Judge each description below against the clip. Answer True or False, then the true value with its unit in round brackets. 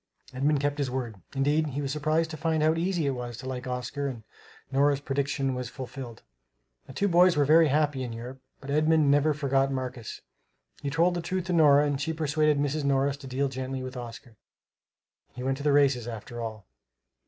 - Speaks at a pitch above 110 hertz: True (140 Hz)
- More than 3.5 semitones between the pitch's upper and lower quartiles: False (2.8 semitones)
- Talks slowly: False (200 wpm)